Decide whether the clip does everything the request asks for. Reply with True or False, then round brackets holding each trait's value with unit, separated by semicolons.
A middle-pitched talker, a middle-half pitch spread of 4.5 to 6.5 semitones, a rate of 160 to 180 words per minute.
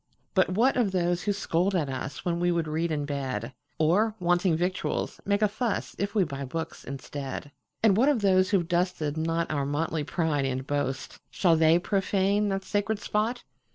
True (175 Hz; 5.0 semitones; 165 wpm)